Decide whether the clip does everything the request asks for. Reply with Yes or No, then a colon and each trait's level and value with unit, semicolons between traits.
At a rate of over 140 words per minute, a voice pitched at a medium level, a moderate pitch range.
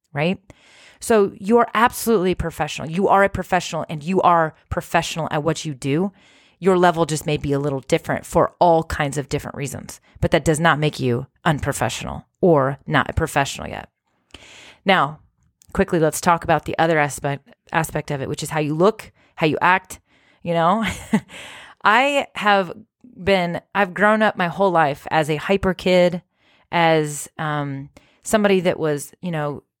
Yes: average, 170 wpm; medium, 165 Hz; average, 4.0 semitones